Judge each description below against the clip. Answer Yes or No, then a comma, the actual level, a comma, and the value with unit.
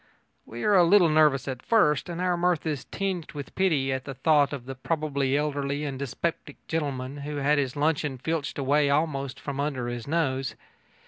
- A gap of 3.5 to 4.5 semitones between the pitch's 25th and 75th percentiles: No, average, 3.0 semitones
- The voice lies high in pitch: No, medium, 145 Hz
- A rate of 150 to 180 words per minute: No, average, 195 wpm